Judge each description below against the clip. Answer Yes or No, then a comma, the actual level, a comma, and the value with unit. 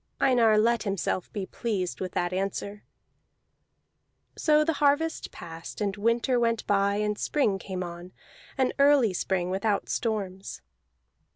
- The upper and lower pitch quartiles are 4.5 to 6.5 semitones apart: No, average, 3.9 semitones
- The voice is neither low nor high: No, high, 210 Hz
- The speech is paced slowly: Yes, slow, 130 wpm